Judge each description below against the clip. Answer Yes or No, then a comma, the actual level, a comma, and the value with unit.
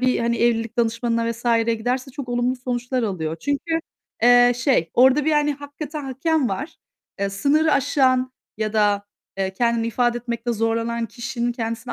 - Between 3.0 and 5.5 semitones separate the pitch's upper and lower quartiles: No, narrow, 2.4 semitones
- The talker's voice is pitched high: Yes, high, 240 Hz